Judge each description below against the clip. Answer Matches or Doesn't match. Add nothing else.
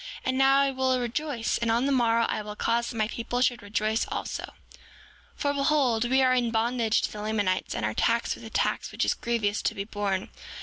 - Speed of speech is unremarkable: Doesn't match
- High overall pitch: Matches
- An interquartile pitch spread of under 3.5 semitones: Matches